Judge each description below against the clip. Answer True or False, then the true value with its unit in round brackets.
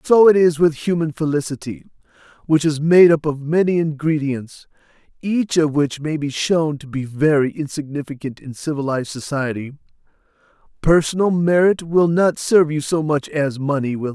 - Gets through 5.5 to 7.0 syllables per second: False (5.0 syllables/s)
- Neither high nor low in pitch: True (150 Hz)